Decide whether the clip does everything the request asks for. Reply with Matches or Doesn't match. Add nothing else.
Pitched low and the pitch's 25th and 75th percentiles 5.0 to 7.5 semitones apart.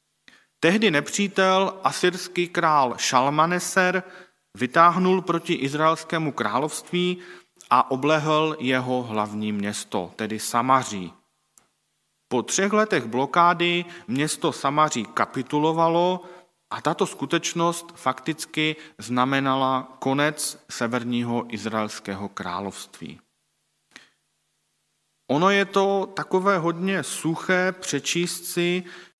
Doesn't match